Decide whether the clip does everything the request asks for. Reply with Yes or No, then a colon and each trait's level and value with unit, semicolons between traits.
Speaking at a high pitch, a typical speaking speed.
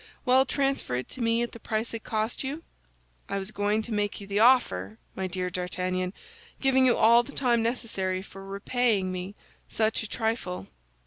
Yes: high, 215 Hz; average, 185 wpm